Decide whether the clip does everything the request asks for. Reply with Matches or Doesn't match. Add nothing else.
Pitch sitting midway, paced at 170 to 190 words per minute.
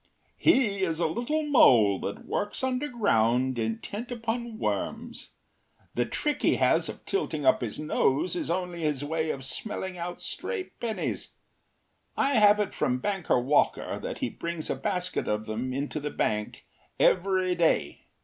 Doesn't match